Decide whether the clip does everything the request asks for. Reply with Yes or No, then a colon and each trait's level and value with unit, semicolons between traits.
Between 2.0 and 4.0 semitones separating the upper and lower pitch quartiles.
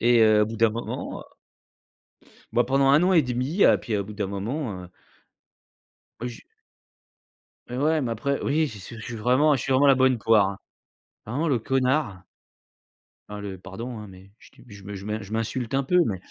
No: average, 4.5 semitones